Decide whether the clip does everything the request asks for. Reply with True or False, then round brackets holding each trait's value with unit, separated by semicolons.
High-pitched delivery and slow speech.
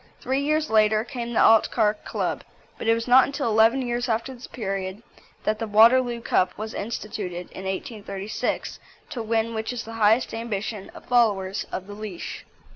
False (225 Hz; 175 wpm)